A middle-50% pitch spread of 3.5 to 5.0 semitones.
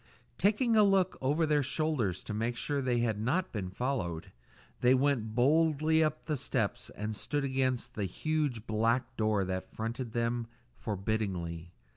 No: wide, 5.4 semitones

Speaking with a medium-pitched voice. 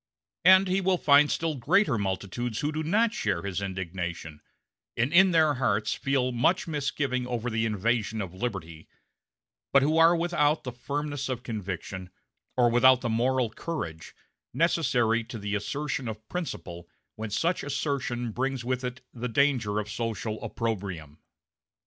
No: low, 120 Hz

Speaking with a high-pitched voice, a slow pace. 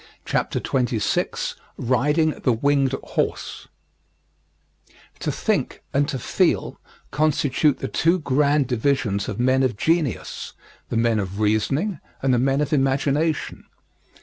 No: low, 135 Hz; slow, 125 wpm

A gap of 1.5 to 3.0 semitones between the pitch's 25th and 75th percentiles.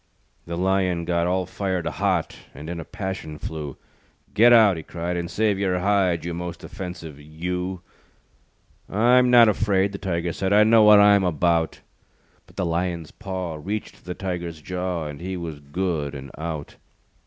Yes: average, 2.7 semitones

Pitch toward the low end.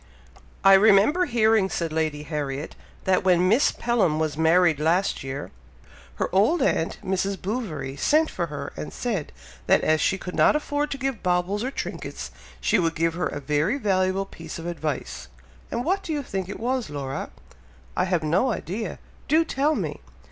No: medium, 185 Hz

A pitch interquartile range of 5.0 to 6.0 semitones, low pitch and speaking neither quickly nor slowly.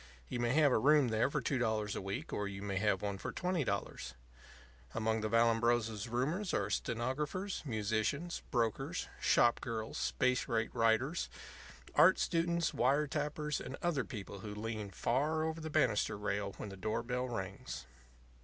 Yes: wide, 5.4 semitones; low, 120 Hz; average, 165 wpm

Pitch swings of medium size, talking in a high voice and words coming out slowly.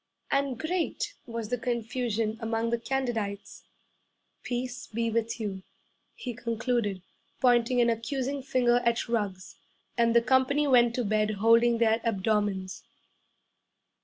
No: narrow, 2.1 semitones; high, 235 Hz; slow, 125 wpm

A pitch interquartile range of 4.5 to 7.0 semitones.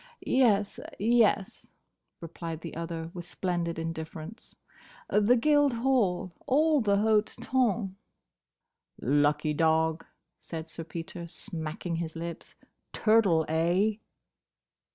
Yes: average, 5.1 semitones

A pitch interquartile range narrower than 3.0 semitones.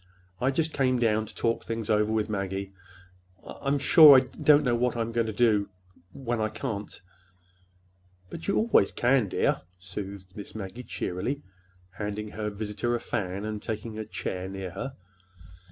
No: average, 3.6 semitones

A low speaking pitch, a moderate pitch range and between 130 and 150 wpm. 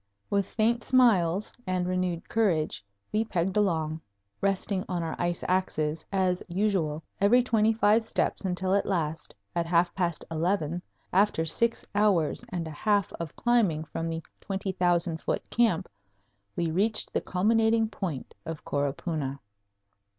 No: medium, 185 Hz; average, 4.0 semitones; average, 140 wpm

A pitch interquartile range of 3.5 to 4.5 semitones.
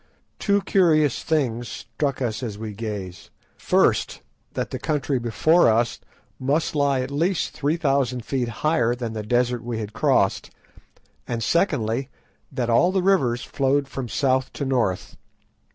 Yes: average, 4.0 semitones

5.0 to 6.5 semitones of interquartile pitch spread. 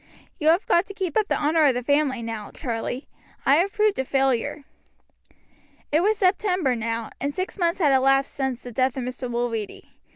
Yes: wide, 5.6 semitones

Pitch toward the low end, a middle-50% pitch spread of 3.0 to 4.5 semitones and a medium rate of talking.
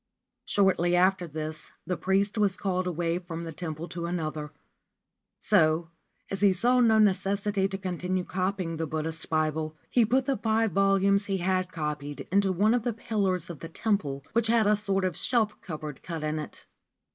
No: medium, 185 Hz; average, 3.7 semitones; average, 180 wpm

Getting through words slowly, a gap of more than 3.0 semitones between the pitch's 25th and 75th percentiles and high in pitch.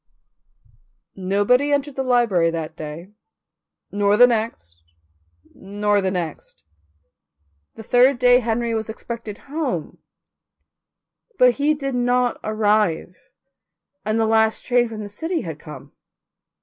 Yes: slow, 120 wpm; average, 3.9 semitones; high, 220 Hz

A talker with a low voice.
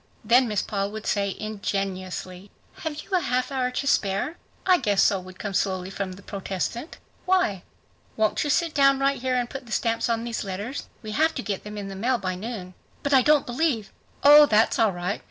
No: high, 220 Hz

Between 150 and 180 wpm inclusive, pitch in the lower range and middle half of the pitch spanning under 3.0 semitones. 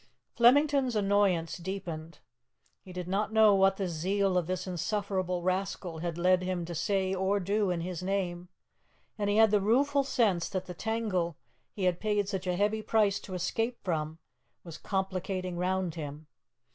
No: average, 170 wpm; high, 190 Hz; narrow, 2.6 semitones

